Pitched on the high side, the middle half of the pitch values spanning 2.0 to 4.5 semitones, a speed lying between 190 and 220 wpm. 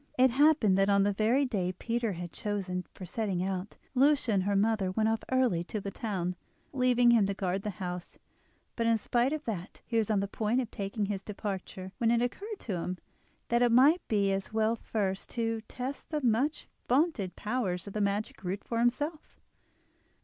Yes: high, 215 Hz; average, 3.9 semitones; average, 200 wpm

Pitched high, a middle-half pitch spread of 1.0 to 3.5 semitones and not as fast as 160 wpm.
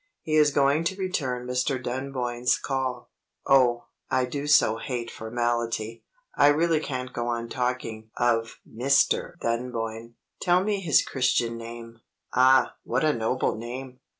No: low, 125 Hz; average, 2.8 semitones; average, 140 wpm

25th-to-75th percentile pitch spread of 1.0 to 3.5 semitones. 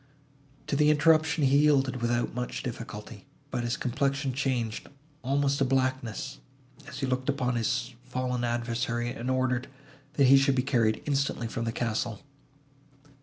Yes: narrow, 2.4 semitones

